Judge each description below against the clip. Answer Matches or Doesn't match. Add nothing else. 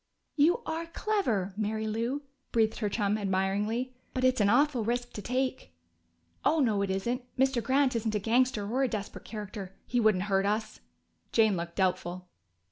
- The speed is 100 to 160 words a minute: Doesn't match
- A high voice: Matches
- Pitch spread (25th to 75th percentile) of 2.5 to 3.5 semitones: Doesn't match